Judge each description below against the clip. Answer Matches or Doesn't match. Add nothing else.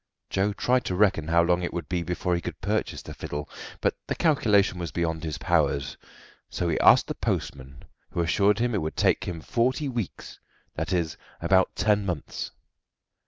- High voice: Doesn't match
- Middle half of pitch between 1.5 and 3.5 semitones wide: Doesn't match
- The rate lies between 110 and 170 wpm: Doesn't match